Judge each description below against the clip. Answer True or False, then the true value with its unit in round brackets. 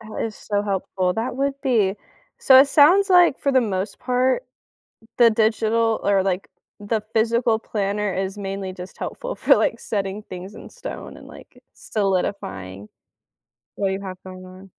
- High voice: True (210 Hz)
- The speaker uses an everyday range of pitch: True (3.5 semitones)